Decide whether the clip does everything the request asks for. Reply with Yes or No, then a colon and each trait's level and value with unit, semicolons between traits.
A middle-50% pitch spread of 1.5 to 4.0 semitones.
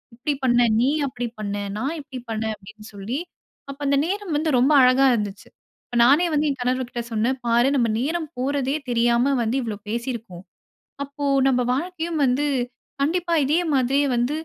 Yes: average, 3.4 semitones